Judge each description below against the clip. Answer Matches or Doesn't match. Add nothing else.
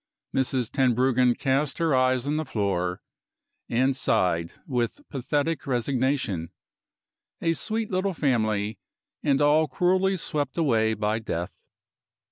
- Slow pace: Matches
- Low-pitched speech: Matches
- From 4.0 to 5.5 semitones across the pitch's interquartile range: Matches